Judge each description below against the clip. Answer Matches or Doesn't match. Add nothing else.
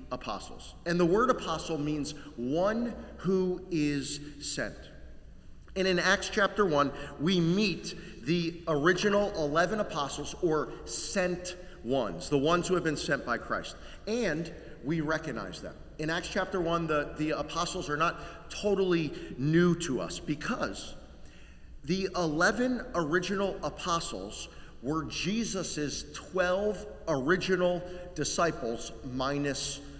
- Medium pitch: Matches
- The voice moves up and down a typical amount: Matches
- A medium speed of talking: Doesn't match